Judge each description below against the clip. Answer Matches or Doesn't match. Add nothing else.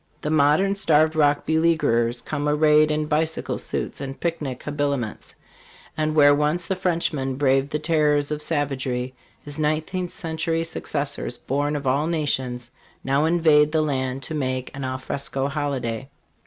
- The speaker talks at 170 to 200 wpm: Doesn't match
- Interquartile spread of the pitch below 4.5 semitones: Matches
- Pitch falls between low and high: Matches